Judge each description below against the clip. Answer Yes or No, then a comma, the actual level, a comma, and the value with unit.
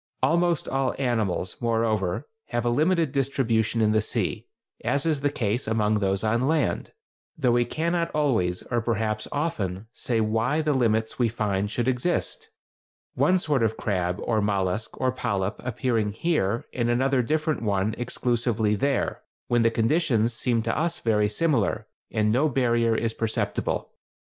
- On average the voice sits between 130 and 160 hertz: No, low, 115 Hz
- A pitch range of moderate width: Yes, average, 4.2 semitones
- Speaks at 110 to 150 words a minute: No, average, 160 wpm